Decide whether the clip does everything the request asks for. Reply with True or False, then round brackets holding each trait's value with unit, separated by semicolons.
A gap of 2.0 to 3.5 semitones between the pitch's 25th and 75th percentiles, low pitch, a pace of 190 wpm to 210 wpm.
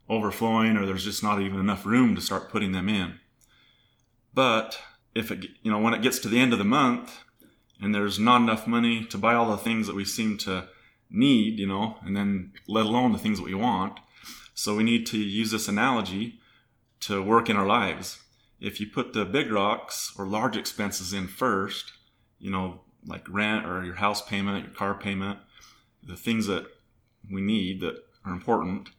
True (2.5 semitones; 105 Hz; 195 wpm)